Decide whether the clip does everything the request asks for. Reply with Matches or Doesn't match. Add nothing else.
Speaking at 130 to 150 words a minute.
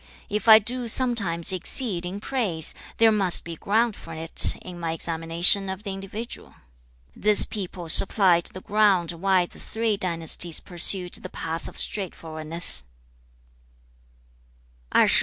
Matches